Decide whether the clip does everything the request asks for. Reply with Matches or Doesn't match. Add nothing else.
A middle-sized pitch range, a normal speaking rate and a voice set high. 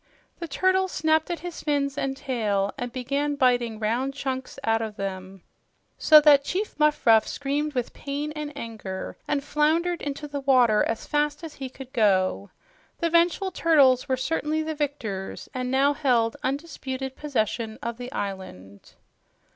Matches